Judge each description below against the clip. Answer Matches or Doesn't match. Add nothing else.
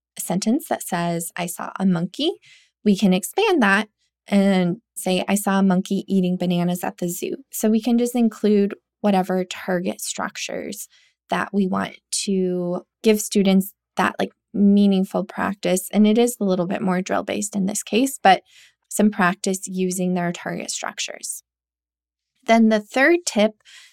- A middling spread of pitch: Matches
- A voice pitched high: Matches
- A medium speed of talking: Matches